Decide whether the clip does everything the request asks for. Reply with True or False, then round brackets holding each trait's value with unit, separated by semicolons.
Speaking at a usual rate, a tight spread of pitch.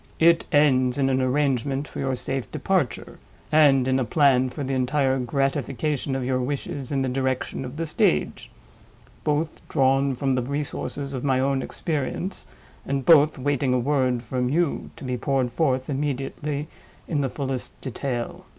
True (165 wpm; 2.0 semitones)